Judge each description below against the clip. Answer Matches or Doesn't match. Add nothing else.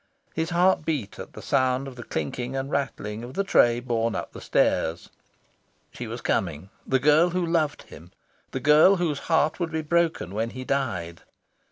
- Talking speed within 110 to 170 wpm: Doesn't match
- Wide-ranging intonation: Matches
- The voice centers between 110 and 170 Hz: Matches